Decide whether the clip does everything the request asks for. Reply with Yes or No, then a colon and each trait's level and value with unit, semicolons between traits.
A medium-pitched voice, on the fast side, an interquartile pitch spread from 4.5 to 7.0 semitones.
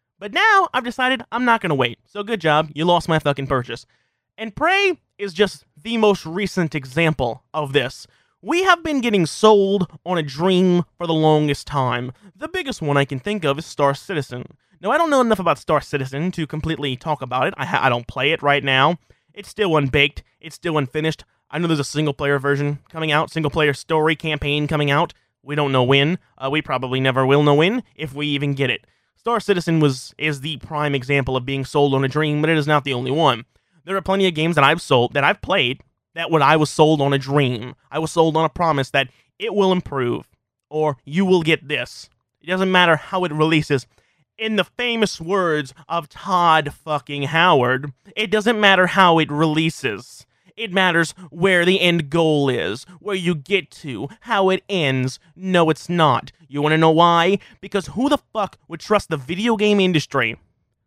Yes: medium, 155 Hz; fast, 210 wpm; average, 4.8 semitones